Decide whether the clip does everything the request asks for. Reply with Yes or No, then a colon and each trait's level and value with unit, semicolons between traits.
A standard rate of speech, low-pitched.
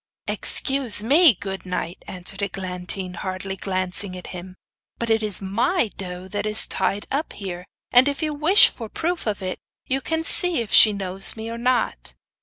No: average, 185 wpm; high, 205 Hz